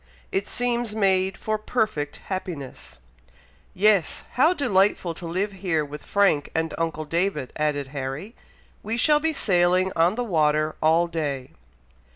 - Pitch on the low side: No, medium, 180 Hz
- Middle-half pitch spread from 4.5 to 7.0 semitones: Yes, average, 5.3 semitones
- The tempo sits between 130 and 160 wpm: Yes, average, 140 wpm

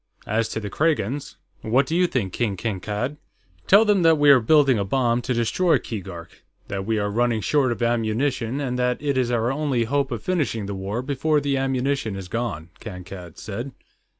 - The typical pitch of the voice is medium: No, low, 120 Hz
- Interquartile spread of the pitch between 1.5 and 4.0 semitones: No, average, 4.8 semitones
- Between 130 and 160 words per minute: No, average, 195 wpm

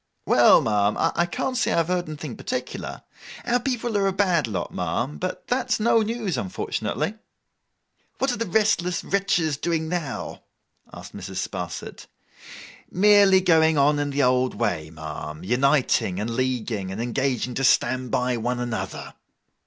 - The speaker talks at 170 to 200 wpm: No, average, 160 wpm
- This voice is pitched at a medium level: Yes, medium, 145 Hz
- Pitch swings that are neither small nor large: No, wide, 8.1 semitones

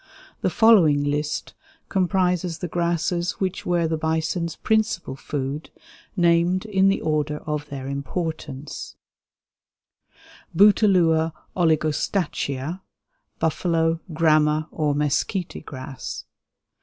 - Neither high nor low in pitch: Yes, medium, 160 Hz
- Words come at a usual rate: No, slow, 95 wpm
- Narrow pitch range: No, average, 3.0 semitones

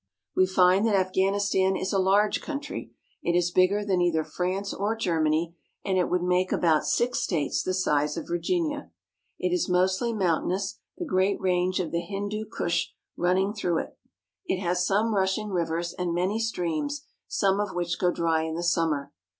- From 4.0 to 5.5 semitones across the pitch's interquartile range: No, average, 2.7 semitones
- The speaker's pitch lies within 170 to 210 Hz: Yes, medium, 185 Hz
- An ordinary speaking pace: Yes, average, 175 wpm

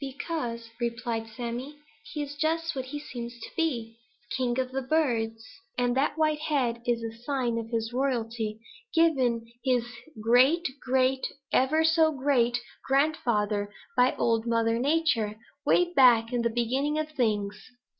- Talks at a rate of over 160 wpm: No, average, 145 wpm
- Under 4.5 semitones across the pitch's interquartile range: Yes, average, 4.0 semitones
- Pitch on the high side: Yes, very high, 250 Hz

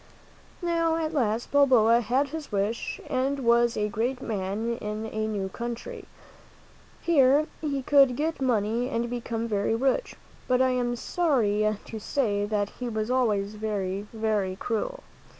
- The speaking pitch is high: Yes, high, 235 Hz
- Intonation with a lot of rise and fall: No, average, 3.8 semitones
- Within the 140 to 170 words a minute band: Yes, average, 150 wpm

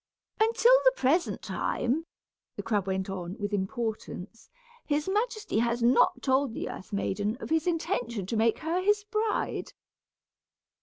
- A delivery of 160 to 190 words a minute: No, average, 145 wpm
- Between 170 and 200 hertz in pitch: No, high, 245 Hz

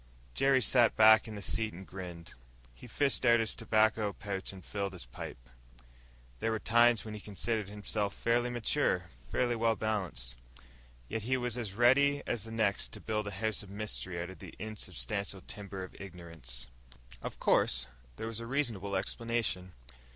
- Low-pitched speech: Yes, low, 105 Hz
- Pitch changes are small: No, average, 3.4 semitones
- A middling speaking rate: Yes, average, 175 wpm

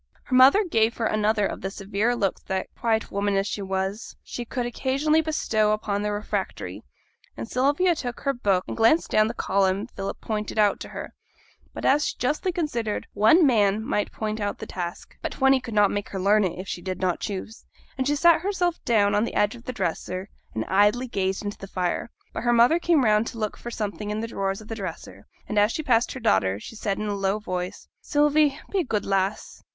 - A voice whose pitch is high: Yes, high, 215 Hz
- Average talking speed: No, fast, 225 wpm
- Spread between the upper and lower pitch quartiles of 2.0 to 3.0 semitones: No, average, 4.0 semitones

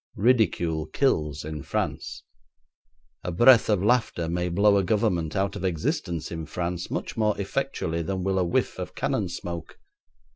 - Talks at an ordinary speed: Yes, average, 155 wpm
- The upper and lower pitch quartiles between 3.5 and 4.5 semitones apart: Yes, average, 3.9 semitones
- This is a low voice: Yes, very low, 90 Hz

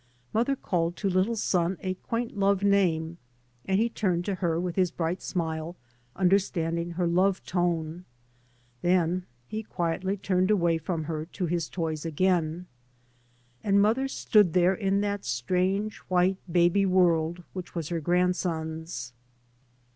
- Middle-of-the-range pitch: Yes, medium, 180 Hz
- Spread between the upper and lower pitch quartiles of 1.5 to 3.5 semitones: Yes, narrow, 2.6 semitones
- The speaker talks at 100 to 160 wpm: Yes, average, 140 wpm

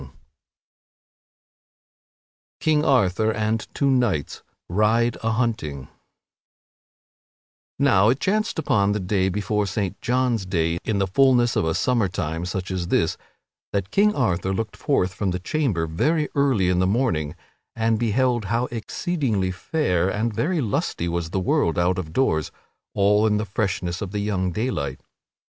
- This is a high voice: No, low, 105 Hz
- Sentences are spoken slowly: No, average, 150 wpm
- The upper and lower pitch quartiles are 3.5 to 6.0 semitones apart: Yes, average, 4.8 semitones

